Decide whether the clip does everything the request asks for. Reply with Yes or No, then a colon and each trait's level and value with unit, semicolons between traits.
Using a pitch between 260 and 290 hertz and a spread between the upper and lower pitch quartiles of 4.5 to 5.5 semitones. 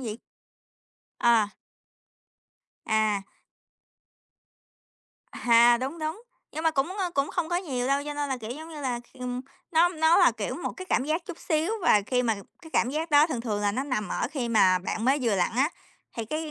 Yes: very high, 270 Hz; average, 5.2 semitones